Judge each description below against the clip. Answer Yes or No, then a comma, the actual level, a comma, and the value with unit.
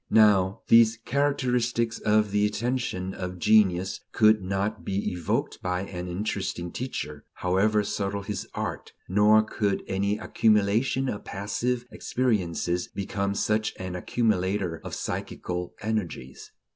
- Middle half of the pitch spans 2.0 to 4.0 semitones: Yes, average, 3.0 semitones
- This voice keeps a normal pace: No, slow, 120 wpm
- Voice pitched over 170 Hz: No, low, 100 Hz